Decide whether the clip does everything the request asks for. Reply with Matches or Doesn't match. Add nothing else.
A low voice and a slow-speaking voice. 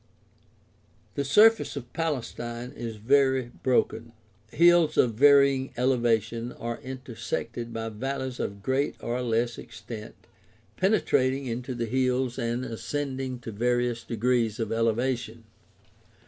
Matches